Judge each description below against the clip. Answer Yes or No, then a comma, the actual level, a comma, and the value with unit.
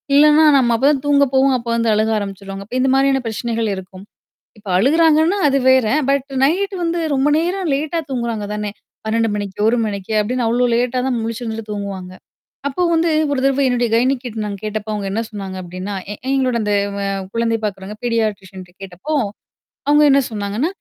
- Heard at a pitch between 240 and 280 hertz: No, high, 230 Hz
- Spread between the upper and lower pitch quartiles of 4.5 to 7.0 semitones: Yes, average, 4.8 semitones